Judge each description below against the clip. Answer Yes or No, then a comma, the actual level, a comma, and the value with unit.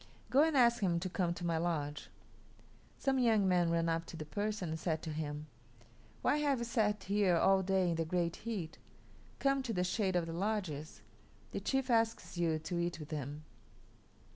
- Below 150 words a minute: No, average, 195 wpm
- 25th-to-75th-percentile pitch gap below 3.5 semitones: No, average, 4.7 semitones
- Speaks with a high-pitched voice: No, medium, 180 Hz